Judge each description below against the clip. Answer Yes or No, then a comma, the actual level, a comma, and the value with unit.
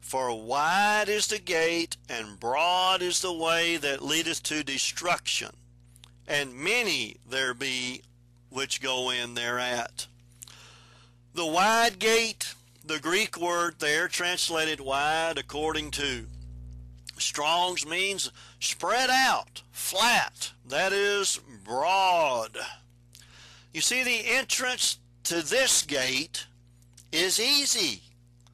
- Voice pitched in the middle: Yes, medium, 145 Hz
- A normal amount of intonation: No, wide, 7.1 semitones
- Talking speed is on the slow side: Yes, slow, 105 wpm